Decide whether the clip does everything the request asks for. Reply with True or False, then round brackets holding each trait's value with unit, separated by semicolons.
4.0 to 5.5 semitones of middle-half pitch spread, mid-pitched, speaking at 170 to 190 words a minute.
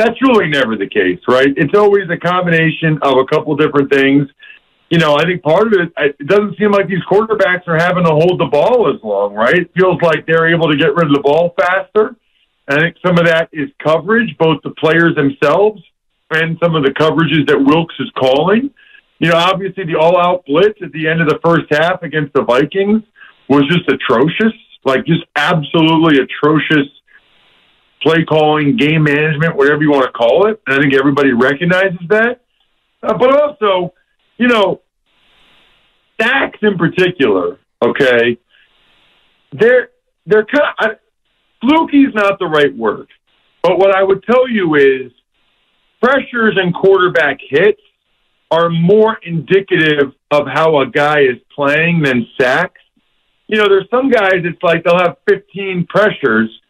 True (5.1 semitones; 170 Hz; 175 wpm)